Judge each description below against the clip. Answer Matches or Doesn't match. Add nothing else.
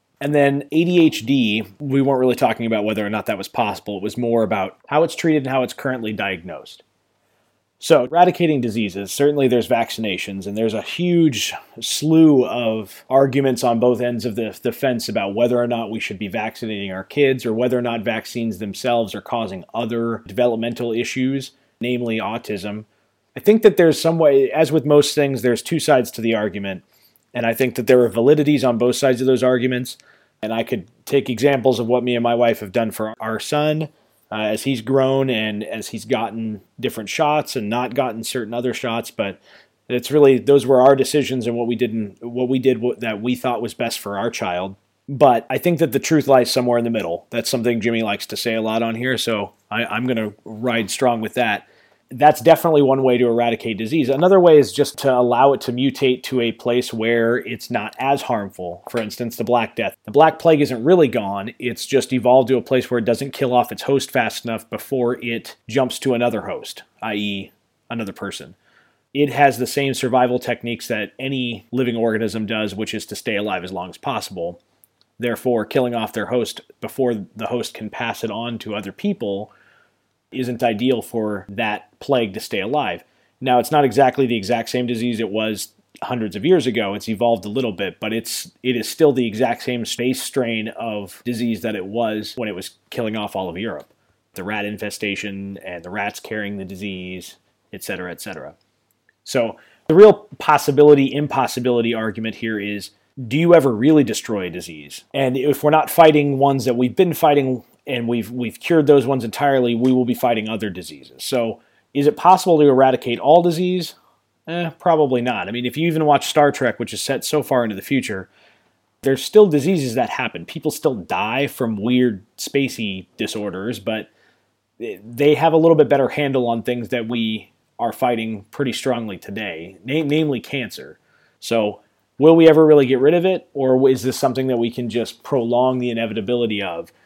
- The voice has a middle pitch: Doesn't match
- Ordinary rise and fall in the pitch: Matches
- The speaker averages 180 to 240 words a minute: Matches